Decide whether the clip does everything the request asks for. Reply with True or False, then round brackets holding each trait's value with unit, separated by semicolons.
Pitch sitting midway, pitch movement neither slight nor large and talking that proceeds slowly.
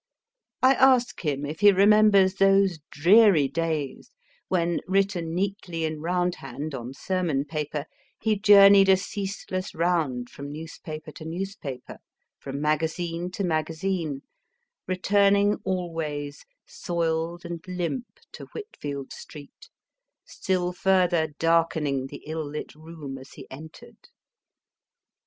True (170 Hz; 4.1 semitones; 115 wpm)